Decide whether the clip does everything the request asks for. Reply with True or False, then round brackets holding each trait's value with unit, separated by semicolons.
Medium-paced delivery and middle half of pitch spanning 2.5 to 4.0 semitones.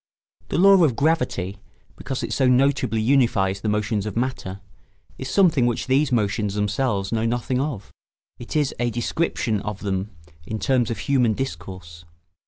False (160 wpm; 4.4 semitones)